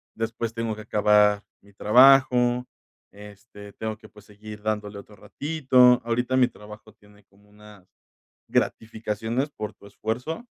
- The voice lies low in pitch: Yes, low, 110 Hz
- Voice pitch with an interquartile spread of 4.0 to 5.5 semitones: No, average, 2.8 semitones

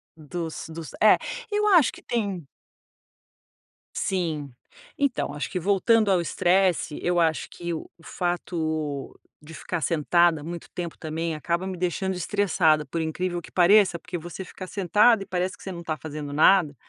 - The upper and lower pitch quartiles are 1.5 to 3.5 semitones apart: Yes, average, 3.0 semitones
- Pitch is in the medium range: Yes, medium, 175 Hz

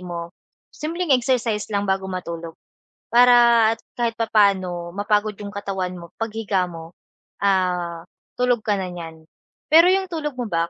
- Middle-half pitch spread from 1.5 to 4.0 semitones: No, average, 5.0 semitones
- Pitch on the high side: Yes, high, 200 Hz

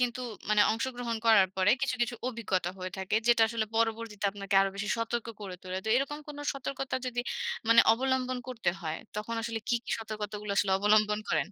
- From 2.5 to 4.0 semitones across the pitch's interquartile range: Yes, average, 2.9 semitones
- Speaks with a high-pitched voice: Yes, high, 225 Hz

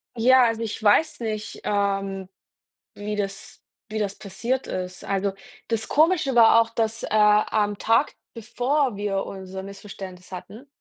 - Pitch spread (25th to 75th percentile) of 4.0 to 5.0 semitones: No, narrow, 2.6 semitones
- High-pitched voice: Yes, high, 210 Hz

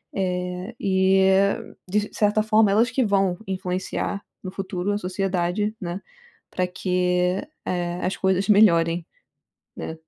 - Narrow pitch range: Yes, narrow, 2.0 semitones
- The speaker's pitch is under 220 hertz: Yes, high, 190 Hz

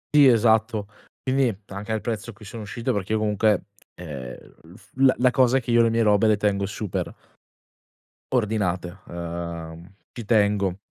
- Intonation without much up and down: No, average, 3.5 semitones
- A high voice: No, low, 105 Hz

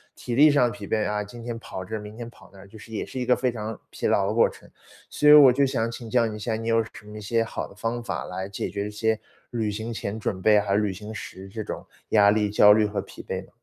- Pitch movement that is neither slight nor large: No, narrow, 2.1 semitones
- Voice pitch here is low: Yes, low, 110 Hz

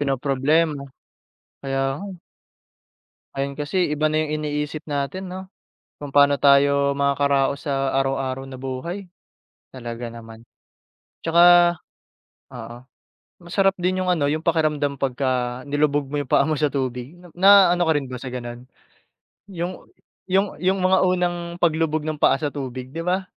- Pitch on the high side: No, medium, 145 Hz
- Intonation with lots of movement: No, average, 4.2 semitones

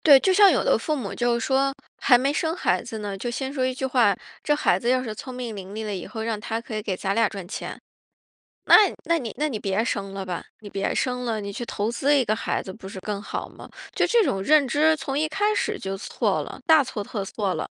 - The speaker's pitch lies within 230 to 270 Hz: Yes, high, 235 Hz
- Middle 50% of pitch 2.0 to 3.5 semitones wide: No, average, 5.2 semitones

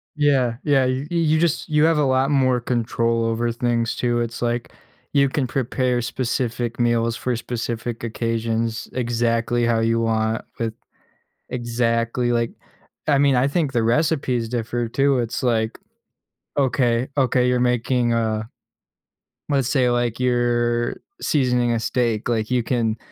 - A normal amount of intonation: No, narrow, 1.9 semitones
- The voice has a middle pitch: No, low, 120 Hz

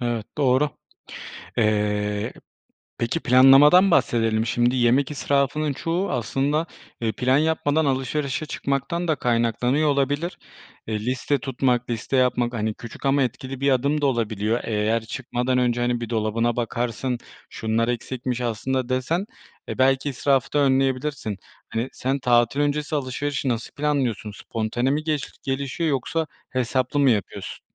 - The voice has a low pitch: Yes, low, 130 Hz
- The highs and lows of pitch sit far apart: No, average, 3.1 semitones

